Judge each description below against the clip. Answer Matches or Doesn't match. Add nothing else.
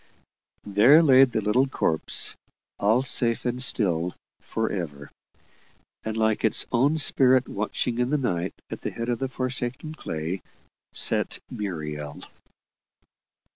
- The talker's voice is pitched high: Doesn't match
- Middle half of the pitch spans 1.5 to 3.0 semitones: Doesn't match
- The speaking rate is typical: Doesn't match